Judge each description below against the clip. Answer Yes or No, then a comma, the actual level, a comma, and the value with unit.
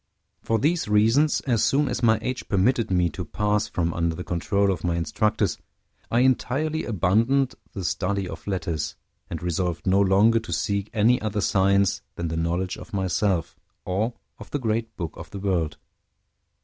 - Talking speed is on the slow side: No, average, 175 wpm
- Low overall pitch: Yes, low, 100 Hz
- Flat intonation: No, average, 4.2 semitones